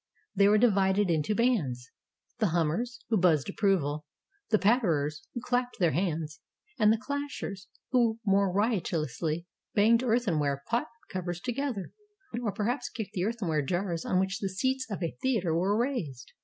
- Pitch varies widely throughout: Yes, wide, 5.7 semitones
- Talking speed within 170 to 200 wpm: No, average, 155 wpm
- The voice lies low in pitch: No, high, 195 Hz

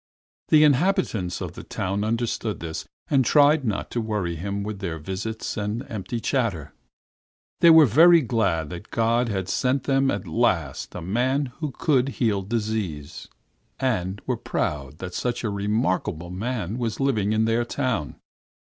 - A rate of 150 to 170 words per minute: Yes, average, 160 wpm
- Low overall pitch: Yes, low, 110 Hz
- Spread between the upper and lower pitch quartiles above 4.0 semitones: Yes, average, 5.1 semitones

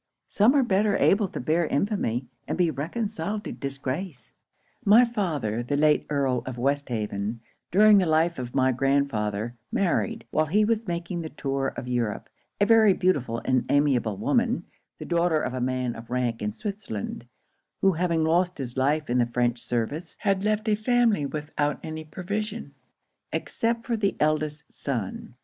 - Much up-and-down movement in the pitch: Yes, wide, 7.6 semitones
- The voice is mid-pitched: Yes, medium, 155 Hz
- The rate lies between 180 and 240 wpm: No, average, 165 wpm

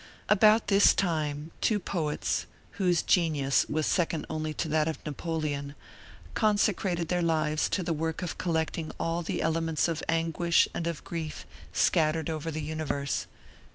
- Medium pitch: Yes, medium, 165 Hz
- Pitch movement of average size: No, narrow, 1.9 semitones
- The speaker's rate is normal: Yes, average, 150 wpm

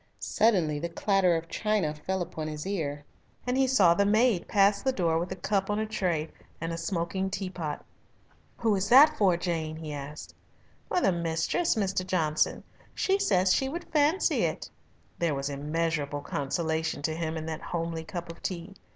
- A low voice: No, medium, 175 Hz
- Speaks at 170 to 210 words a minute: Yes, average, 180 wpm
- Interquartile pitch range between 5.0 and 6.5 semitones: No, average, 4.1 semitones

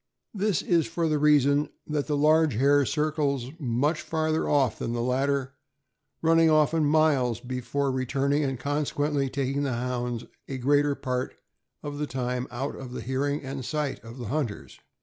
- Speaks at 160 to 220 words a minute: Yes, average, 170 wpm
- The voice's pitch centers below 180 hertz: Yes, medium, 140 Hz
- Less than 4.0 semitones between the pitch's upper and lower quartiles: Yes, average, 2.8 semitones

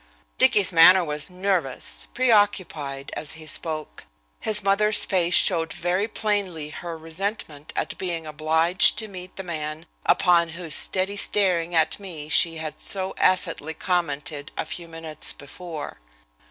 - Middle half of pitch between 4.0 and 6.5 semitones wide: No, average, 3.3 semitones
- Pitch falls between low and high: Yes, medium, 170 Hz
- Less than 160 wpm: Yes, average, 140 wpm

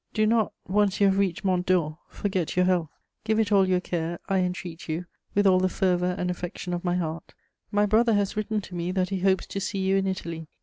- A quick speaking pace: Yes, fast, 235 wpm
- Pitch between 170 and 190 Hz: Yes, medium, 185 Hz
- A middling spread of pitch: No, narrow, 2.0 semitones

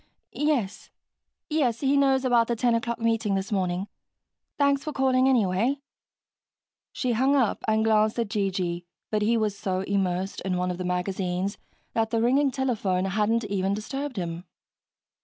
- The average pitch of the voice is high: Yes, high, 220 Hz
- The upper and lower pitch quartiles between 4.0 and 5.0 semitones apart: Yes, average, 4.6 semitones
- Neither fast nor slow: Yes, average, 160 wpm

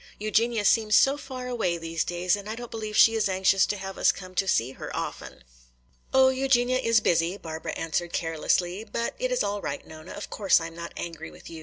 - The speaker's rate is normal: No, fast, 220 wpm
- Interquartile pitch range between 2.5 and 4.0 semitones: No, average, 5.2 semitones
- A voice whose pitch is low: No, high, 200 Hz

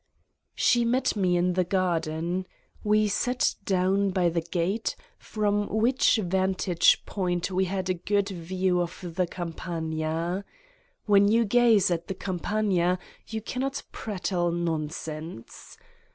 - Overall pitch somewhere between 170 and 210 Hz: Yes, medium, 185 Hz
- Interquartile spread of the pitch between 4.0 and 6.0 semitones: No, average, 3.0 semitones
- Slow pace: Yes, slow, 125 wpm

